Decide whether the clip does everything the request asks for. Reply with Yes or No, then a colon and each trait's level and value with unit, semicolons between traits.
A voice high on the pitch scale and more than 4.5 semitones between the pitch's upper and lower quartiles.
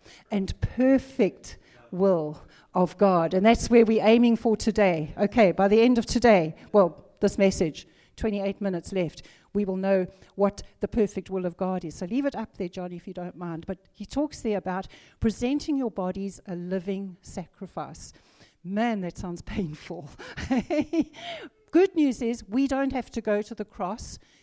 No: high, 200 Hz; average, 4.0 semitones